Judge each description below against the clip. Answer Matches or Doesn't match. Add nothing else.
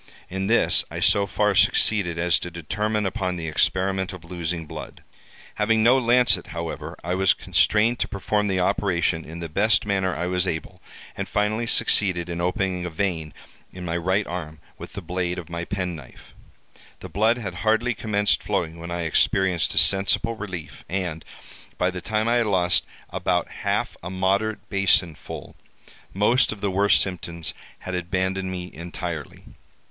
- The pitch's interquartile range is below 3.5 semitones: Matches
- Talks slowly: Doesn't match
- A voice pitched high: Doesn't match